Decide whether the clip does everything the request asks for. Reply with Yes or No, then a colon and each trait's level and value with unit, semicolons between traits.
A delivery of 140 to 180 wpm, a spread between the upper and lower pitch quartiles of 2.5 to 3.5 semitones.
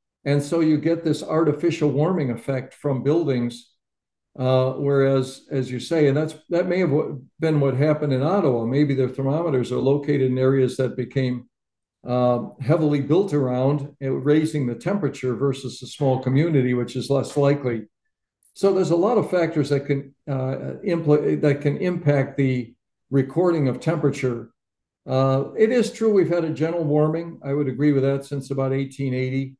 Yes: average, 170 wpm; average, 2.8 semitones